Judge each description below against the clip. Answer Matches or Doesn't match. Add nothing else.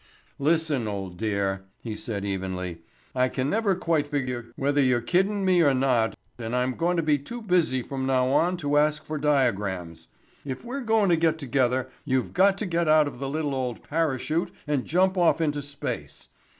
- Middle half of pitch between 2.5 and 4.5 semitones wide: Doesn't match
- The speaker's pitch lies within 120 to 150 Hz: Matches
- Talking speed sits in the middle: Matches